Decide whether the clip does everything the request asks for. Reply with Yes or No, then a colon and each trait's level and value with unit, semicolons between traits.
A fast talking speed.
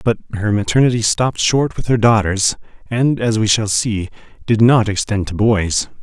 No: average, 180 wpm